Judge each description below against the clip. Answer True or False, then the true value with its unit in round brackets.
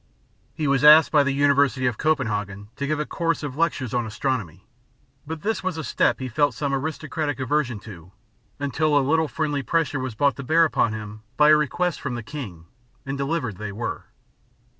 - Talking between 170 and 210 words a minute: True (195 wpm)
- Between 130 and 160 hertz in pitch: True (140 Hz)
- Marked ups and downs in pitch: False (4.2 semitones)